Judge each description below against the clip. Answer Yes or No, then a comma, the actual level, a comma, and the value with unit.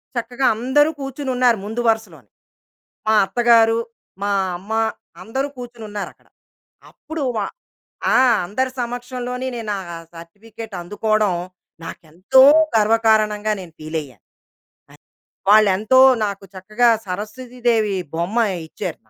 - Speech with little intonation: No, average, 3.3 semitones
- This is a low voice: No, high, 220 Hz